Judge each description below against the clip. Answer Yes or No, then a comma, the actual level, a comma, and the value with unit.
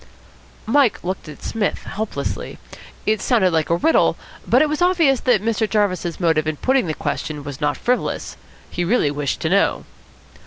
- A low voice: No, high, 200 Hz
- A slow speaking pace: No, average, 170 wpm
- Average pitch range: No, wide, 7.8 semitones